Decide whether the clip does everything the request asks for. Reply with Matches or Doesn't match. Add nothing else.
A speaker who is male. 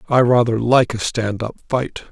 Matches